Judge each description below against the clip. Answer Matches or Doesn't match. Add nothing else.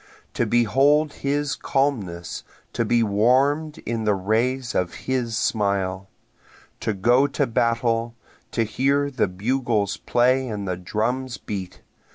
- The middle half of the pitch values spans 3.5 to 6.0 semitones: Matches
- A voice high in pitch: Doesn't match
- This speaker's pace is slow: Matches